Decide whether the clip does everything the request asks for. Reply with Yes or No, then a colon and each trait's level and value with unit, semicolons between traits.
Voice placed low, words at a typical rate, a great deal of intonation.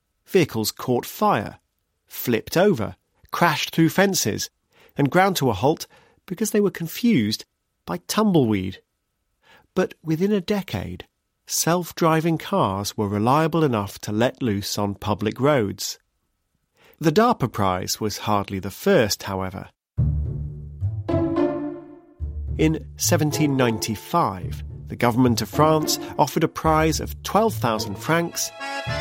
No: low, 125 Hz; slow, 115 wpm; wide, 8.4 semitones